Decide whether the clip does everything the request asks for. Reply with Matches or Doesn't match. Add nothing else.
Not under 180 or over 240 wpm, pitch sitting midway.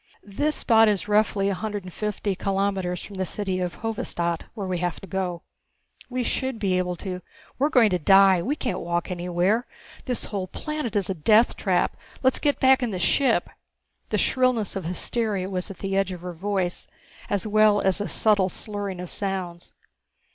Doesn't match